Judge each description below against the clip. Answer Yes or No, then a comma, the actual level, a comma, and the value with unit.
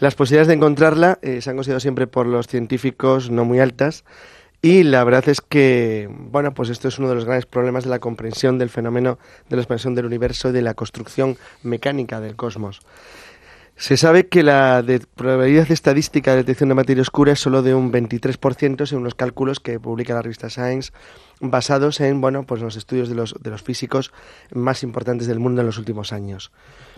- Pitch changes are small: Yes, narrow, 2.3 semitones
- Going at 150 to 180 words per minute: No, average, 200 wpm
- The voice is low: Yes, low, 130 Hz